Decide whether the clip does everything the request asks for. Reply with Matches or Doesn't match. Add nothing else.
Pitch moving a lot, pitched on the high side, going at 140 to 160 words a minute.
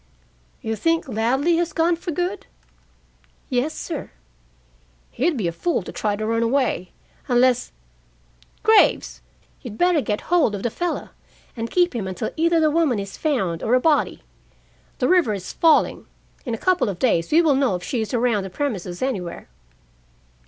Doesn't match